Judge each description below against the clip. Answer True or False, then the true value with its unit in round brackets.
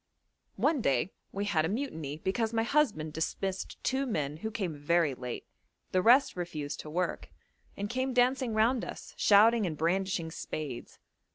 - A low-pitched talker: False (190 Hz)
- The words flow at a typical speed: True (160 wpm)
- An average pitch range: False (6.8 semitones)